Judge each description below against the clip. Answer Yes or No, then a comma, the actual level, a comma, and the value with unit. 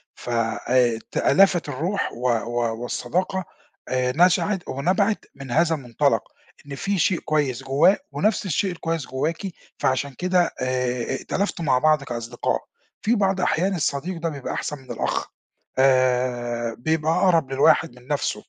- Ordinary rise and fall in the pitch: No, wide, 5.8 semitones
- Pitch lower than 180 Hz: Yes, medium, 140 Hz